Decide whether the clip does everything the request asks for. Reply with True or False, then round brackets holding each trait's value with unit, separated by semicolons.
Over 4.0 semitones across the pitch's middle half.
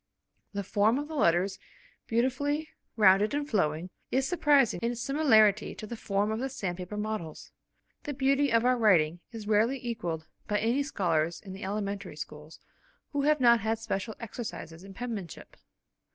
True (4.9 semitones)